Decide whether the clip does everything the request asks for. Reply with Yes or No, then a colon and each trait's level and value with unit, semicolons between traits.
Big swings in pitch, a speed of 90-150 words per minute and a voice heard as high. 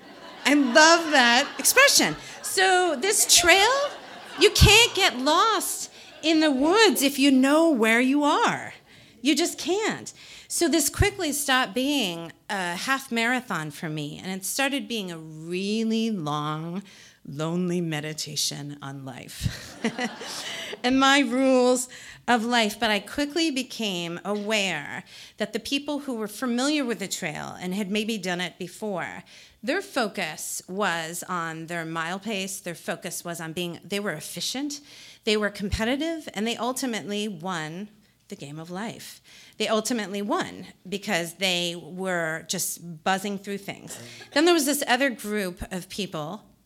Yes: wide, 7.5 semitones; average, 145 wpm; high, 215 Hz